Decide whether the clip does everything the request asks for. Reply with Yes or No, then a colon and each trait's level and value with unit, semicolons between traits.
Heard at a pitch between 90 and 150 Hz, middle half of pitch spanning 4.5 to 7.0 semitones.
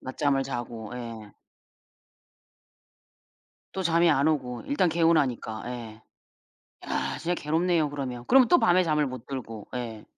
Yes: low, 135 Hz; wide, 5.6 semitones